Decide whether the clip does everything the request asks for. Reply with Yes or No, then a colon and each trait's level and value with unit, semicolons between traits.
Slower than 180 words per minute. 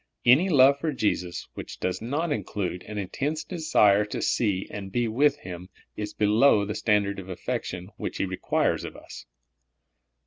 Yes: average, 165 wpm